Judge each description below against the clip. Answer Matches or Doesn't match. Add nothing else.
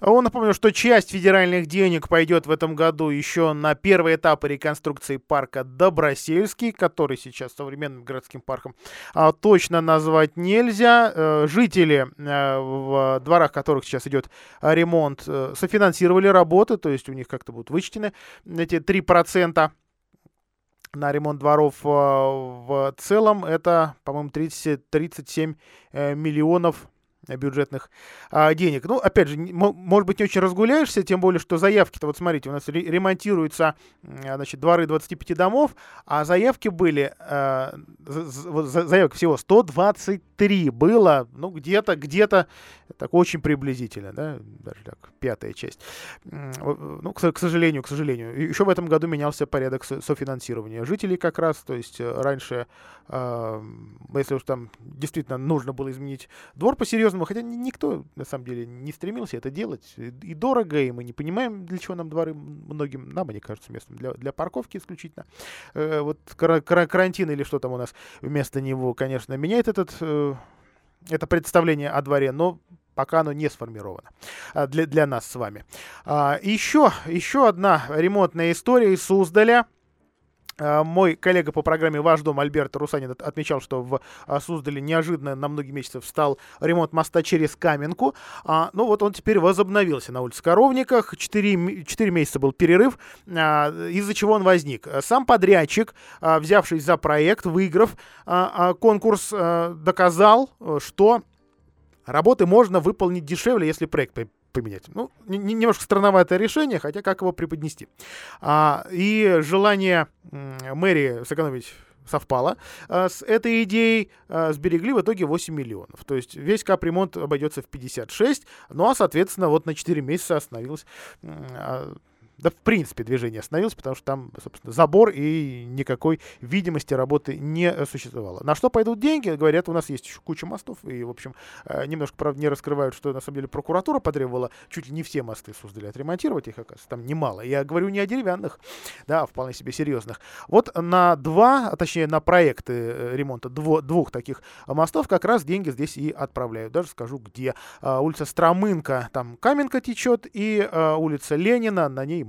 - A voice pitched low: Doesn't match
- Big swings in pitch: Doesn't match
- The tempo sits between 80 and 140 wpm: Doesn't match